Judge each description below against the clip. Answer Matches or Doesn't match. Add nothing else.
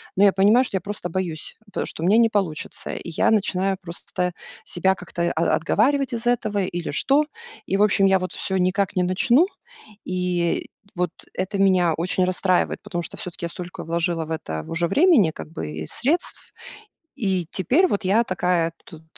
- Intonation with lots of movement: Doesn't match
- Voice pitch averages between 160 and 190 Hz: Matches